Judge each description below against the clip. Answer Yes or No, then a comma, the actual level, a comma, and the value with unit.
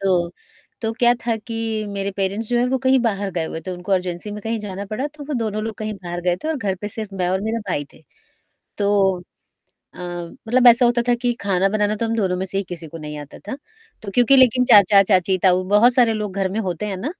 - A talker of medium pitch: No, high, 205 Hz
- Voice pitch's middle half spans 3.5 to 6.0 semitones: Yes, average, 3.8 semitones